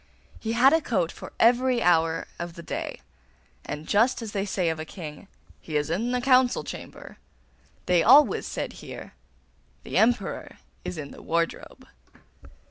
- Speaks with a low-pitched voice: No, high, 195 Hz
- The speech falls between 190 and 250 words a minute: No, average, 160 wpm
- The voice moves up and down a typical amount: No, wide, 6.8 semitones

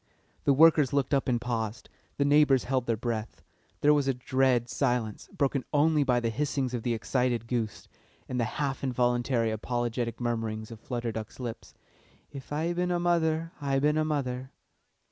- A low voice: Yes, low, 125 Hz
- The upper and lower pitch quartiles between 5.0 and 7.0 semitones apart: No, average, 3.4 semitones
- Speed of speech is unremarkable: Yes, average, 175 wpm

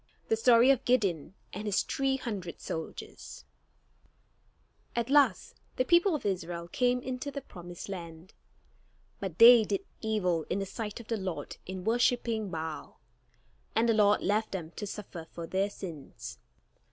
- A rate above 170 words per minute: No, average, 150 wpm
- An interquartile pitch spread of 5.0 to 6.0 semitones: Yes, wide, 5.4 semitones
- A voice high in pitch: Yes, high, 205 Hz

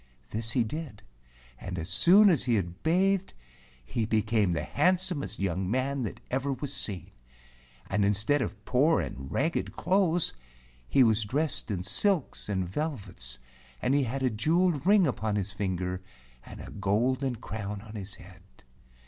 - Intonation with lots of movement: Yes, wide, 7.1 semitones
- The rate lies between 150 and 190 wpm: Yes, average, 160 wpm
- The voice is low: Yes, low, 115 Hz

